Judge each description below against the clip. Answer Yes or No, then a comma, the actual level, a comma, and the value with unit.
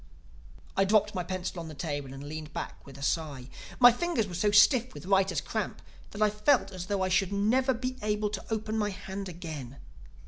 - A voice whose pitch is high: Yes, high, 195 Hz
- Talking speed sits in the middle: No, fast, 210 wpm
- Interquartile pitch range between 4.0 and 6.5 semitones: Yes, average, 4.5 semitones